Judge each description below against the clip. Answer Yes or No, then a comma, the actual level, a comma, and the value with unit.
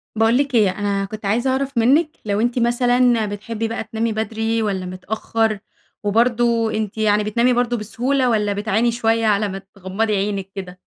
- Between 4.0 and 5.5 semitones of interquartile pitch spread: No, narrow, 2.5 semitones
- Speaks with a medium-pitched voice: No, high, 220 Hz